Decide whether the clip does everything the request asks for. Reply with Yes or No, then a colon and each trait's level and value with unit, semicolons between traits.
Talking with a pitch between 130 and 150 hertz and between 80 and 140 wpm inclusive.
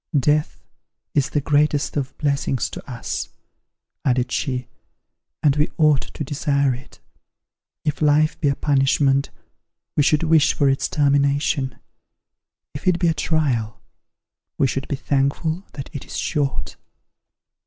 Yes: medium, 140 Hz; slow, 135 wpm